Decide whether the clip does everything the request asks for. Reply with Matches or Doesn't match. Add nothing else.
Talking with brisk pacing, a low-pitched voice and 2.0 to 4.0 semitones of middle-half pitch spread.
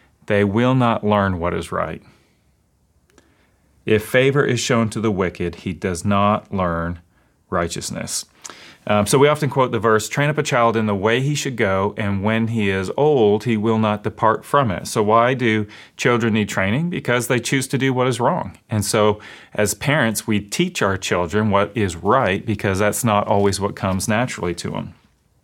Doesn't match